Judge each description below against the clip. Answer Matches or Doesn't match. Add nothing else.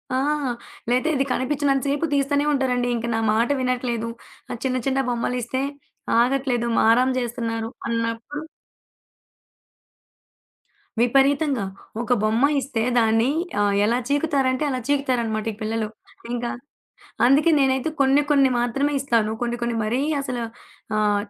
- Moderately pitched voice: Doesn't match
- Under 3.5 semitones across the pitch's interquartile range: Matches